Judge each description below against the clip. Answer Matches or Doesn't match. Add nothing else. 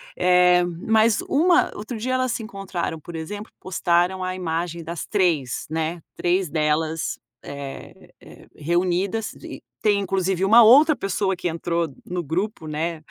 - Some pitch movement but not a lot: Matches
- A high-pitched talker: Doesn't match